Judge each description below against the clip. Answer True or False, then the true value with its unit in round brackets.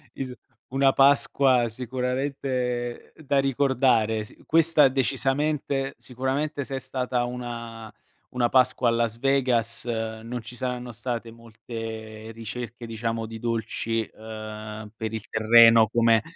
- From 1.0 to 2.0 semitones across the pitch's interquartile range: False (2.8 semitones)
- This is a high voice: False (120 Hz)